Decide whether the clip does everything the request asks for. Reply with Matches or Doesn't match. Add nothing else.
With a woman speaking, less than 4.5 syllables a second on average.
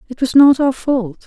Doesn't match